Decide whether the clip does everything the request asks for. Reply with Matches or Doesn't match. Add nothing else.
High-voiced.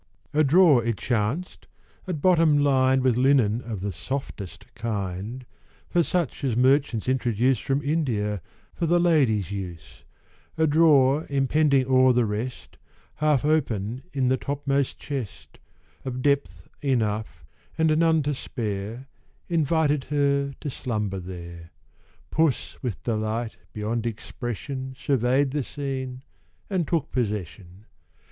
Doesn't match